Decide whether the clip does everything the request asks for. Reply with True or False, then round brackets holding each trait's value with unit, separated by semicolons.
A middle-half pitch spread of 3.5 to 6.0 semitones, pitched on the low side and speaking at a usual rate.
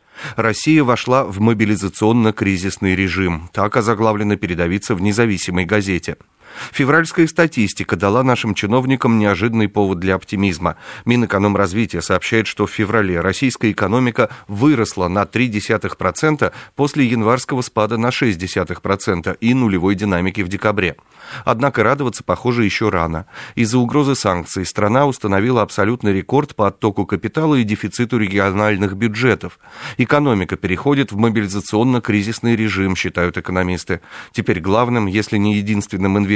True (3.8 semitones; 105 Hz; 120 wpm)